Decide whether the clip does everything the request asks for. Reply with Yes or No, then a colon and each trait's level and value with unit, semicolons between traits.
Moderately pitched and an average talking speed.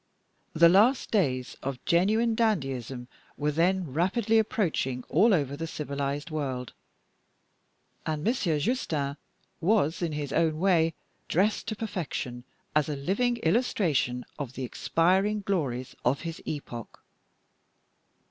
No: medium, 160 Hz; slow, 120 wpm